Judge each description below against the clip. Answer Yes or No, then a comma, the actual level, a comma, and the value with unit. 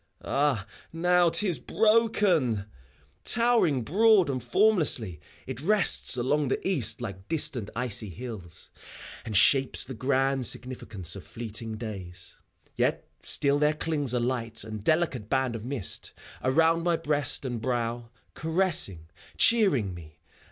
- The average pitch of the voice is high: No, low, 130 Hz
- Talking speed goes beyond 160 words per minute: No, slow, 135 wpm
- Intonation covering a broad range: Yes, wide, 6.6 semitones